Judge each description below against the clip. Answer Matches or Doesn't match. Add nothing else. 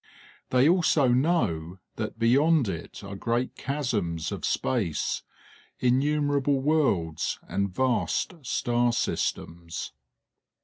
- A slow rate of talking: Matches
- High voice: Doesn't match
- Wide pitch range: Matches